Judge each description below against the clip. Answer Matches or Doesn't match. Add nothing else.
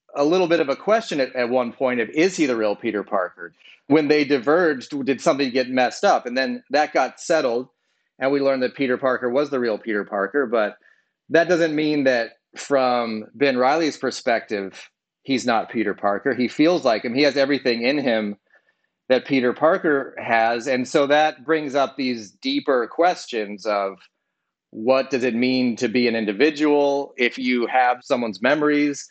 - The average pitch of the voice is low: Matches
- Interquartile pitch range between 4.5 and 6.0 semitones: Doesn't match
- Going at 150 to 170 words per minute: Doesn't match